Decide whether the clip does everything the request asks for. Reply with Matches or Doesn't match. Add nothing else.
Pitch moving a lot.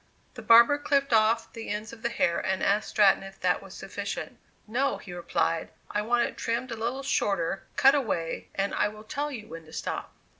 Doesn't match